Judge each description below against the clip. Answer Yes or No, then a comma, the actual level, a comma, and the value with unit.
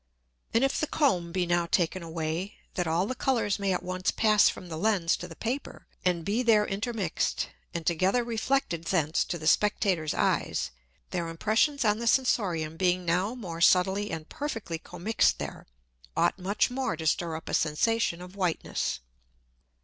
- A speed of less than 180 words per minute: Yes, average, 170 wpm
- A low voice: No, medium, 185 Hz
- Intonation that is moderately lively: Yes, average, 4.7 semitones